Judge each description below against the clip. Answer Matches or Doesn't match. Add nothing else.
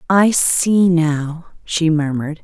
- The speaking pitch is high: Doesn't match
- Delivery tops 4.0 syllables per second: Doesn't match